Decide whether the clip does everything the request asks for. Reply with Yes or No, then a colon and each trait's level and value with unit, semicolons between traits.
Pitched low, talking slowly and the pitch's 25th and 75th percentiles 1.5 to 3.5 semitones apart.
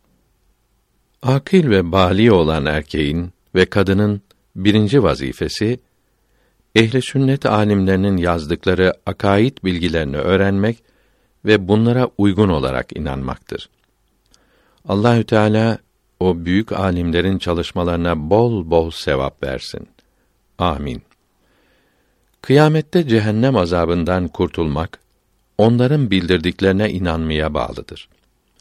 No: very low, 95 Hz; slow, 85 wpm; average, 4.2 semitones